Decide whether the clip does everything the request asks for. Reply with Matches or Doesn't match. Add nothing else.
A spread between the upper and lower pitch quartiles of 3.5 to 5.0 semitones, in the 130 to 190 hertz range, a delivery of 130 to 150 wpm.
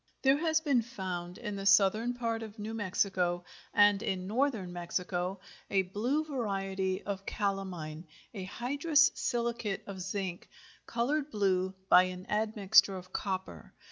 Doesn't match